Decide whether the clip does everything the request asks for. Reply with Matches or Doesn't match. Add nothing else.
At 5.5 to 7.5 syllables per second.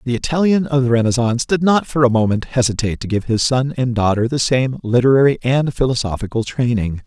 Matches